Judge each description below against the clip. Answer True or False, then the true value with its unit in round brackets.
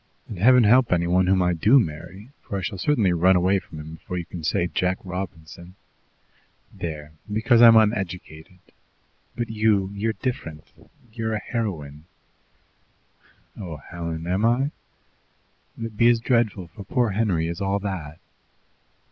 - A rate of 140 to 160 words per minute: True (155 wpm)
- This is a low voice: True (95 Hz)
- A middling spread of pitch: True (4.5 semitones)